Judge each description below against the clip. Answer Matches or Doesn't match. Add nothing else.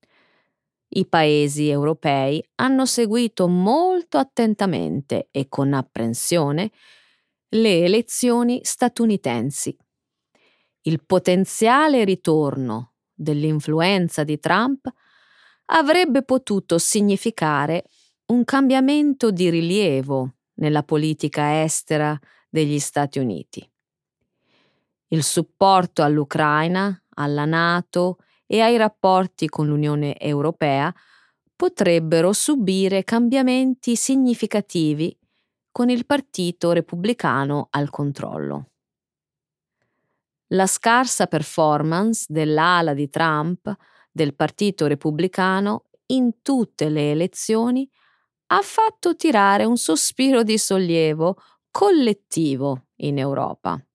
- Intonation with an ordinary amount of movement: Doesn't match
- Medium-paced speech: Doesn't match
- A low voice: Doesn't match